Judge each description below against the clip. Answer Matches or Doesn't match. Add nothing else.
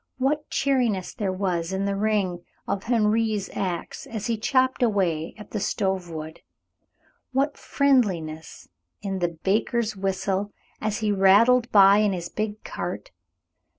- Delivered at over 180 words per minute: Doesn't match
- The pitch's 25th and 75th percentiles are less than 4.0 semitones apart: Matches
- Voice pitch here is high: Matches